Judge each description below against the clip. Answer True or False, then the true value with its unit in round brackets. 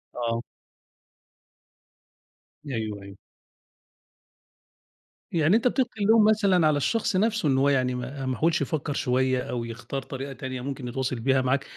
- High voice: False (135 Hz)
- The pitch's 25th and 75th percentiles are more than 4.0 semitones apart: True (4.7 semitones)